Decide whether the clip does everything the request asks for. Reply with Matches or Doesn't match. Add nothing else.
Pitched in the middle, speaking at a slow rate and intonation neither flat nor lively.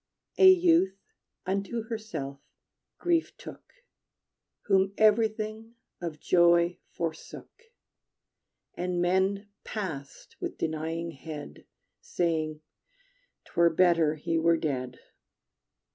Matches